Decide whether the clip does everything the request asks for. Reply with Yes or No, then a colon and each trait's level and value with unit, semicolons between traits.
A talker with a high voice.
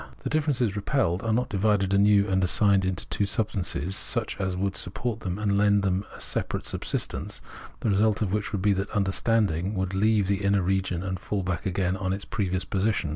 No: low, 100 Hz